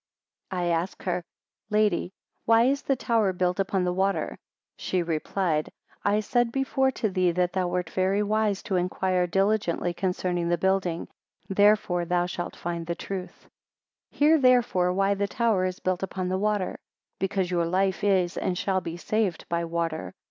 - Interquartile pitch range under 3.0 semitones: Yes, narrow, 2.6 semitones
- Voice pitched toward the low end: No, medium, 185 Hz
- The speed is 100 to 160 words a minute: No, average, 170 wpm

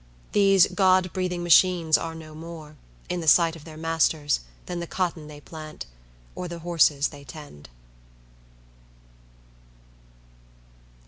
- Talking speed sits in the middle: No, slow, 125 wpm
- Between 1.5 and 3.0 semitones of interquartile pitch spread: Yes, narrow, 2.4 semitones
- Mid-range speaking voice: Yes, medium, 165 Hz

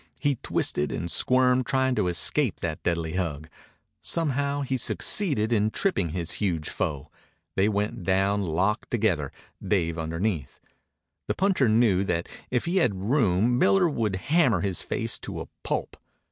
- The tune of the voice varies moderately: No, wide, 6.7 semitones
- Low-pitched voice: Yes, low, 100 Hz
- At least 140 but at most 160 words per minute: Yes, average, 150 wpm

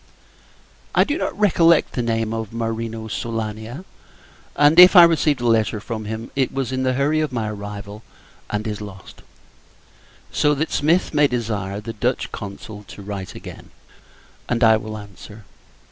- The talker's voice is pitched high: No, low, 115 Hz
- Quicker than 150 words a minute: Yes, average, 175 wpm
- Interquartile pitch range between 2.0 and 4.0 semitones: No, average, 4.5 semitones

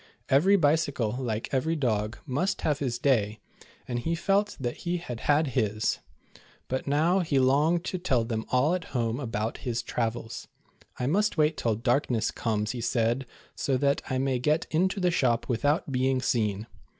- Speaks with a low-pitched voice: Yes, low, 130 Hz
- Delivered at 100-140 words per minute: No, average, 175 wpm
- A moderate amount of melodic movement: Yes, average, 5.0 semitones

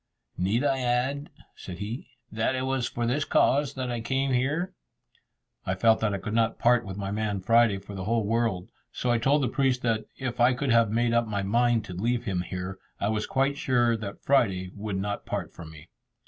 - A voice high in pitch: No, low, 115 Hz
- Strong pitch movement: No, average, 3.8 semitones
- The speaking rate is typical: No, fast, 220 wpm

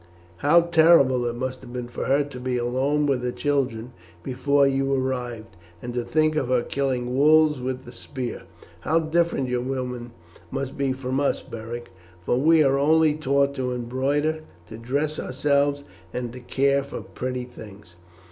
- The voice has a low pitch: Yes, low, 130 Hz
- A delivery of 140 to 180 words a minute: Yes, average, 170 wpm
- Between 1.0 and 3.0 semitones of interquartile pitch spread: Yes, average, 2.7 semitones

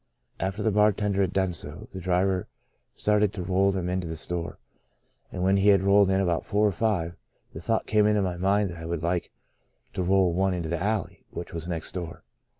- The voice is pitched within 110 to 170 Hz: No, very low, 95 Hz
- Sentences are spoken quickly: Yes, fast, 220 wpm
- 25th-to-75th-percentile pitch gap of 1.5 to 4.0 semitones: Yes, narrow, 2.6 semitones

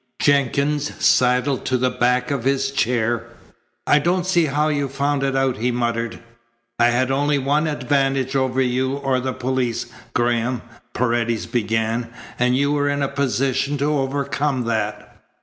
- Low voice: Yes, low, 130 Hz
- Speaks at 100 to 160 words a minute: Yes, average, 155 wpm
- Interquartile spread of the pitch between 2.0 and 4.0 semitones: Yes, narrow, 2.5 semitones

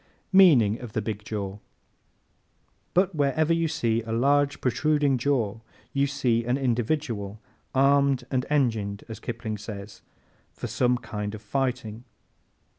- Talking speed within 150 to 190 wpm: No, slow, 135 wpm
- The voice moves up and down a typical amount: Yes, average, 4.3 semitones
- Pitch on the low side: Yes, low, 125 Hz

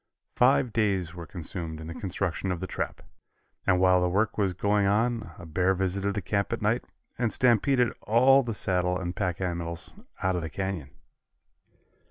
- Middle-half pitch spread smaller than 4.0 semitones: Yes, average, 3.0 semitones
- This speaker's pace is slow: No, average, 180 wpm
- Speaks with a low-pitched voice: Yes, very low, 95 Hz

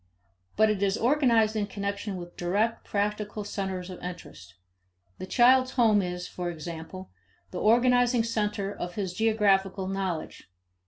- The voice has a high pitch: Yes, high, 200 Hz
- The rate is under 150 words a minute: Yes, average, 140 wpm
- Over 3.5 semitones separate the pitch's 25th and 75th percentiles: No, average, 3.2 semitones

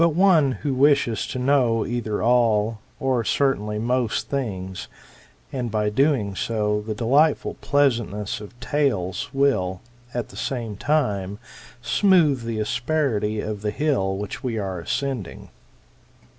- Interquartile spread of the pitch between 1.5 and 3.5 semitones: No, average, 4.7 semitones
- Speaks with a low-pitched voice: Yes, low, 115 Hz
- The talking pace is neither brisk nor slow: No, slow, 130 wpm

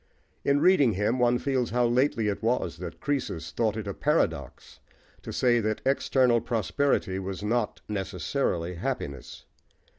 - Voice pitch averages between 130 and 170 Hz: No, low, 115 Hz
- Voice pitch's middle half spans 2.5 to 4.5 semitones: Yes, average, 4.2 semitones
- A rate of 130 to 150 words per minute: Yes, average, 145 wpm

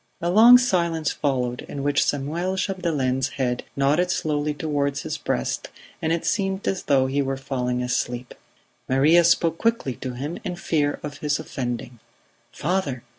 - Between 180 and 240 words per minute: No, average, 155 wpm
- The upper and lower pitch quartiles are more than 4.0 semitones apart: Yes, average, 4.4 semitones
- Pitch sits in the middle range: Yes, medium, 145 Hz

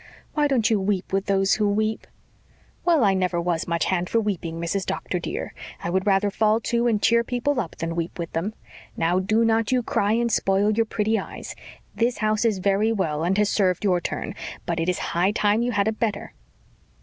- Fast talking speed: Yes, fast, 215 wpm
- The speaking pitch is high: Yes, high, 205 Hz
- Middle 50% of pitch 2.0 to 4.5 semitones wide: Yes, average, 3.5 semitones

